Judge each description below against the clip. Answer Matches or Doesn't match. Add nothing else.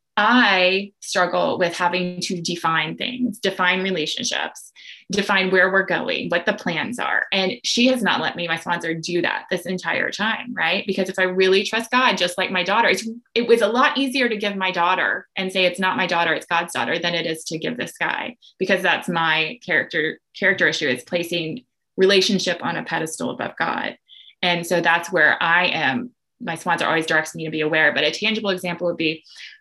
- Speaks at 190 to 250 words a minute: Matches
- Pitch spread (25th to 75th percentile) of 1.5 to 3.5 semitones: Matches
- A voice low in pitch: Doesn't match